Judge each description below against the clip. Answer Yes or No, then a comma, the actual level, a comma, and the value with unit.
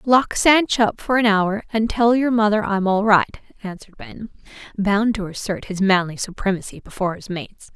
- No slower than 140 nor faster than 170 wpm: No, average, 185 wpm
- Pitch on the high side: Yes, high, 210 Hz